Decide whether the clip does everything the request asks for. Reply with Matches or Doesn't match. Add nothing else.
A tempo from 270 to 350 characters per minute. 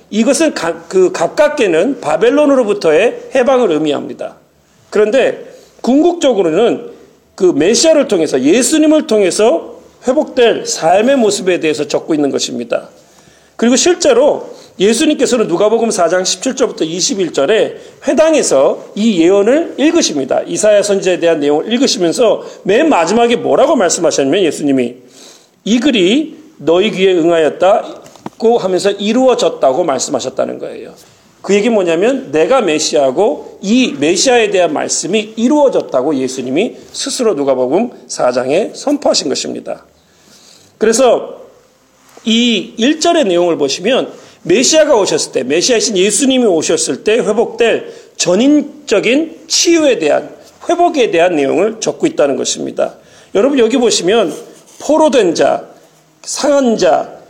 Matches